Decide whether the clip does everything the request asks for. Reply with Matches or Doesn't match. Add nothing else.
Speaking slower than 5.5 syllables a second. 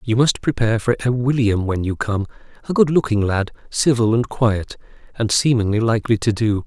Matches